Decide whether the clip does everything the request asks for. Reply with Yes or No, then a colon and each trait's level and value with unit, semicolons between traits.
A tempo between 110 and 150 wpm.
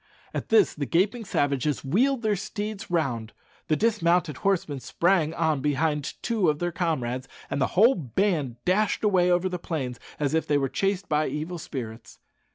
No: average, 170 wpm